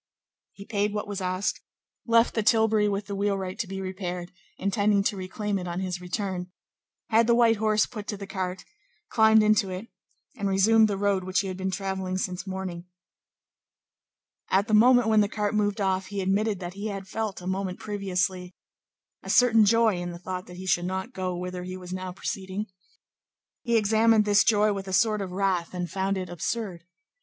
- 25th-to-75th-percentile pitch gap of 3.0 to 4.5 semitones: No, narrow, 2.4 semitones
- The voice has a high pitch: Yes, high, 195 Hz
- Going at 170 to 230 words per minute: Yes, average, 195 wpm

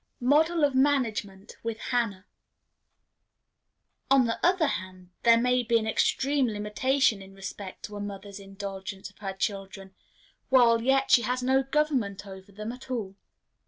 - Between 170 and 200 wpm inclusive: No, average, 150 wpm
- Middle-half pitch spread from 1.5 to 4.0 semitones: No, average, 4.9 semitones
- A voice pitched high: Yes, high, 225 Hz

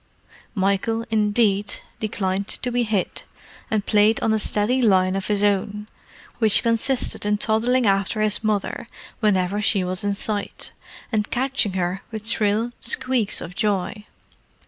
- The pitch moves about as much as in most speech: No, narrow, 2.1 semitones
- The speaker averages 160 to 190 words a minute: No, average, 145 wpm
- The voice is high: Yes, high, 210 Hz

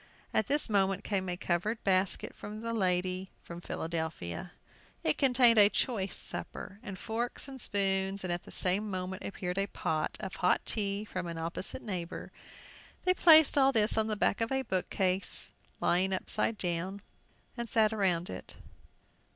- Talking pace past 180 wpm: No, average, 160 wpm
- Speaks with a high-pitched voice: Yes, high, 195 Hz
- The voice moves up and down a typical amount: Yes, average, 3.1 semitones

